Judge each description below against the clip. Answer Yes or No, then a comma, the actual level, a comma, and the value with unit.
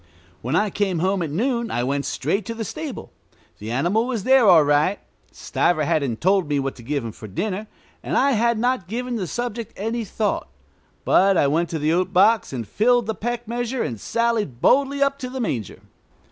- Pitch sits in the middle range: No, high, 200 Hz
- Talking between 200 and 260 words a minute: Yes, fast, 205 wpm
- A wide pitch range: Yes, wide, 7.6 semitones